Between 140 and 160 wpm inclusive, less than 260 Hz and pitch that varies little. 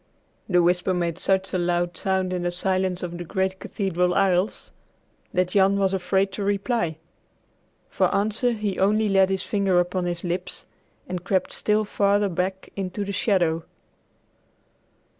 Yes: average, 155 wpm; high, 190 Hz; narrow, 1.9 semitones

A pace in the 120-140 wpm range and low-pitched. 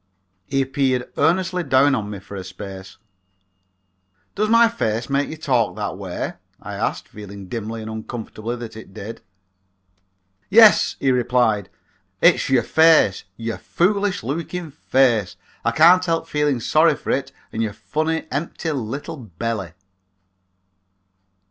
Yes: slow, 135 wpm; low, 125 Hz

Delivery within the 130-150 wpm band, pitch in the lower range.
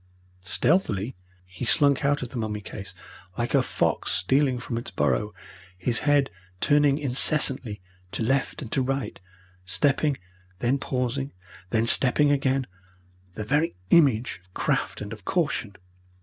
Yes: average, 140 wpm; low, 130 Hz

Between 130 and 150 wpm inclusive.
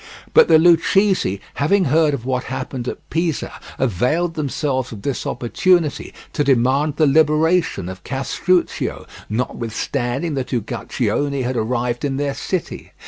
Yes: average, 140 wpm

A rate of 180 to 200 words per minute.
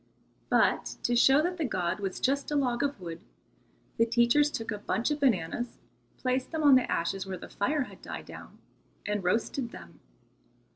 Yes: average, 185 wpm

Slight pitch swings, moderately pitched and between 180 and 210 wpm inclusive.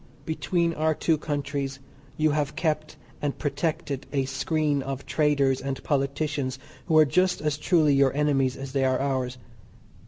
No: narrow, 2.3 semitones; medium, 145 Hz; average, 155 wpm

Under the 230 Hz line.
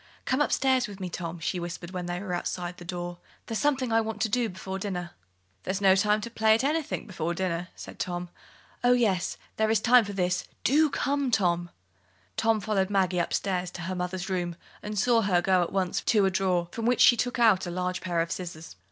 Yes: high, 190 Hz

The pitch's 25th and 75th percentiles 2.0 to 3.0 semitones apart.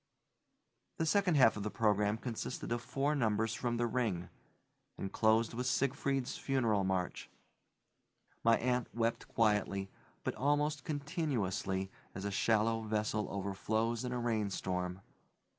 No: average, 3.7 semitones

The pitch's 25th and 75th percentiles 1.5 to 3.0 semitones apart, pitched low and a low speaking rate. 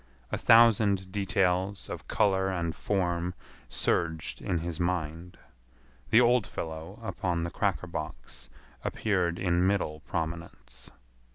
Yes: average, 2.7 semitones; very low, 90 Hz; slow, 115 wpm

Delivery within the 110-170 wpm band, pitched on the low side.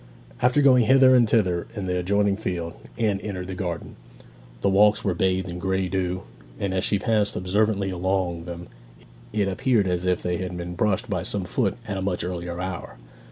No: average, 195 wpm; very low, 95 Hz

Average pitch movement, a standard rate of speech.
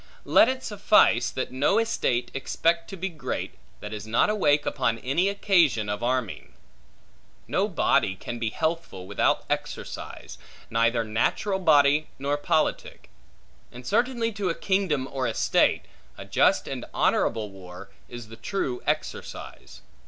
No: wide, 8.7 semitones; average, 145 wpm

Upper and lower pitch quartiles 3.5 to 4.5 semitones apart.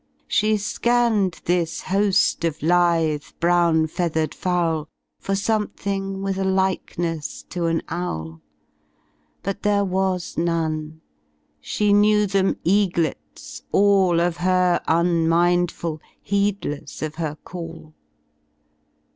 No: average, 3.1 semitones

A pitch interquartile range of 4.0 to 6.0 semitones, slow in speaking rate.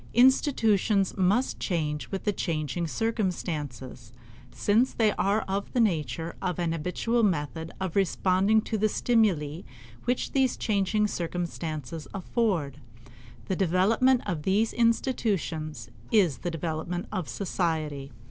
Yes: average, 5.1 semitones; slow, 120 wpm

